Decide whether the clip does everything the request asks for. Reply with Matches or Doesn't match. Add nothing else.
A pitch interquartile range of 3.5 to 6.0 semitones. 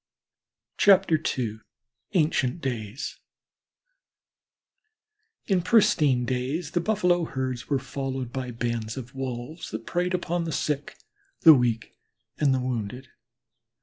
Matches